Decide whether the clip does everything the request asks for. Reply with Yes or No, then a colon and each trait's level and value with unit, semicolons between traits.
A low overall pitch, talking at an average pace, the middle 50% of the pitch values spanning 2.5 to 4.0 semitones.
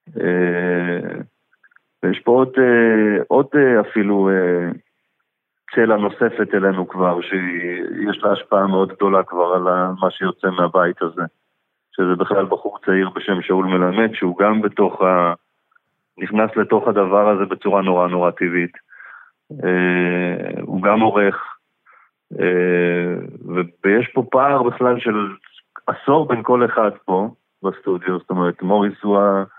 Yes: very low, 95 Hz; average, 130 wpm; average, 3.1 semitones